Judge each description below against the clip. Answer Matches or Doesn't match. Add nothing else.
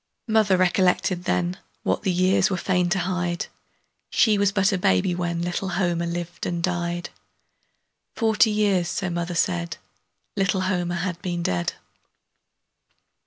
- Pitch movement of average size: Doesn't match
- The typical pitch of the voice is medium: Matches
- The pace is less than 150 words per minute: Matches